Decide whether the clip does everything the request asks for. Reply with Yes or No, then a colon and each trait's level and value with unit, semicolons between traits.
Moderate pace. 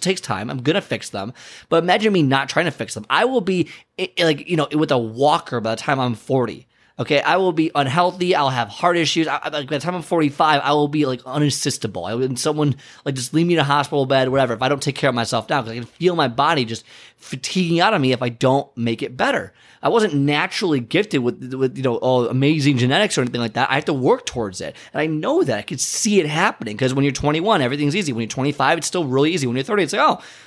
No: fast, 265 wpm